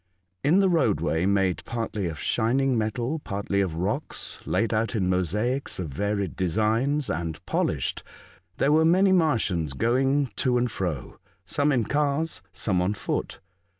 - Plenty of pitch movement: Yes, wide, 7.0 semitones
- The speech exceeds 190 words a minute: No, average, 150 wpm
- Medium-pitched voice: No, low, 110 Hz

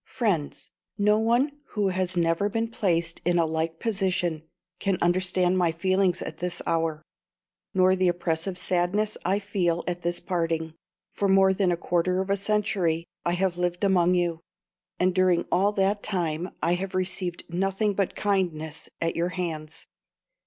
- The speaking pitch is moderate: Yes, medium, 180 Hz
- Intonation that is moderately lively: No, narrow, 2.3 semitones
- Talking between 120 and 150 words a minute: No, average, 160 wpm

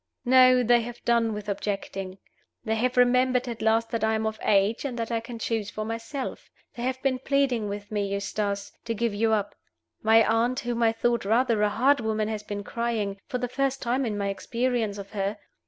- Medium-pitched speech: No, high, 225 Hz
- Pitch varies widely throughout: No, average, 2.7 semitones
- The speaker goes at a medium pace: No, fast, 210 wpm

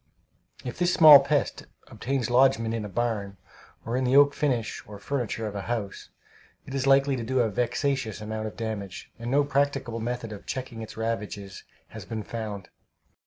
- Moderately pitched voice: No, low, 115 Hz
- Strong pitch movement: No, average, 3.8 semitones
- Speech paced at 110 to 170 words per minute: No, average, 180 wpm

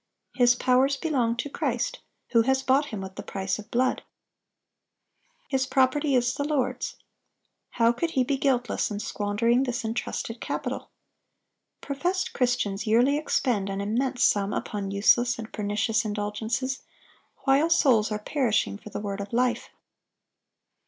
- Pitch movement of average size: Yes, average, 4.0 semitones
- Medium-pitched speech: No, high, 240 Hz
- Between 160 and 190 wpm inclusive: No, average, 145 wpm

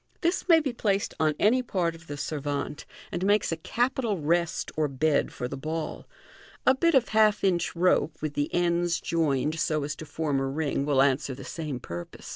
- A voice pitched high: No, medium, 160 Hz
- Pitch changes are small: No, average, 5.3 semitones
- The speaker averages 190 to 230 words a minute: Yes, average, 200 wpm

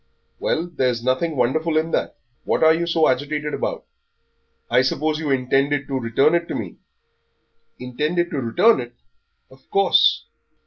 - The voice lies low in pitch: No, medium, 150 Hz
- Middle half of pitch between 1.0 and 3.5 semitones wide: No, average, 4.0 semitones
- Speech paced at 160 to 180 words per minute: No, average, 150 wpm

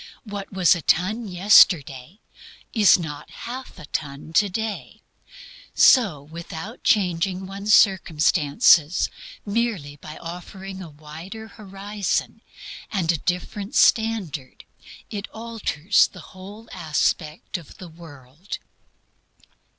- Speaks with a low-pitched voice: No, medium, 185 Hz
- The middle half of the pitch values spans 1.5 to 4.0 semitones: No, average, 4.6 semitones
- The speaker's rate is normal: No, slow, 105 wpm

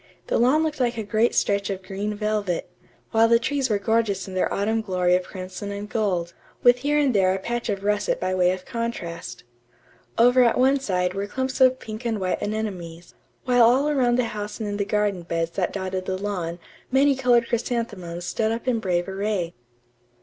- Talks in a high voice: Yes, high, 210 Hz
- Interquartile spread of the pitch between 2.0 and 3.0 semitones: No, average, 4.3 semitones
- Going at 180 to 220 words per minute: Yes, average, 200 wpm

